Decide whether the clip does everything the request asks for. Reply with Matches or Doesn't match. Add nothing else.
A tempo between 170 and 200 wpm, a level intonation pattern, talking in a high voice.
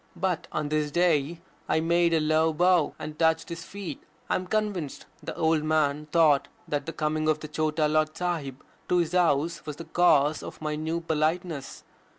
Doesn't match